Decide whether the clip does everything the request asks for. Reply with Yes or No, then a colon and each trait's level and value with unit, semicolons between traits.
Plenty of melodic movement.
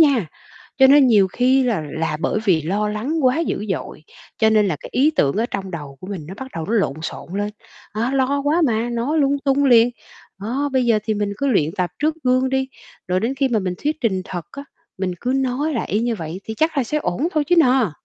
Yes: wide, 5.7 semitones